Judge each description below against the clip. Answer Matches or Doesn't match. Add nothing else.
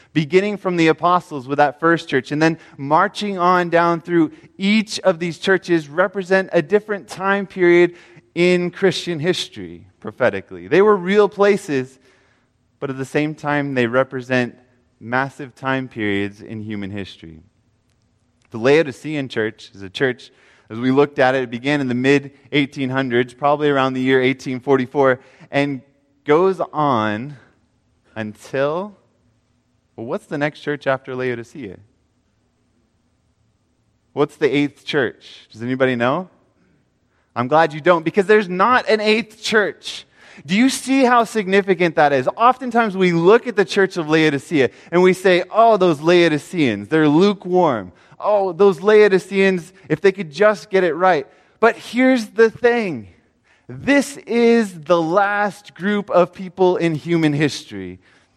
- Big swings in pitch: Matches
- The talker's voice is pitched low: Doesn't match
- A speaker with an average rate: Matches